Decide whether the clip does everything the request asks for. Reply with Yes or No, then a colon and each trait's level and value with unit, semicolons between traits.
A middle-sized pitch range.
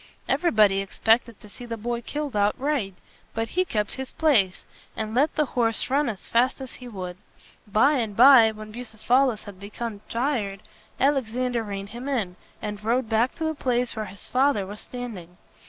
Yes: average, 3.7 semitones